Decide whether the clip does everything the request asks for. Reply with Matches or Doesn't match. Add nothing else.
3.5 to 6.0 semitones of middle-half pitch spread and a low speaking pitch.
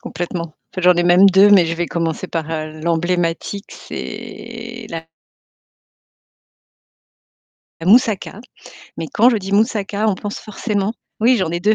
Doesn't match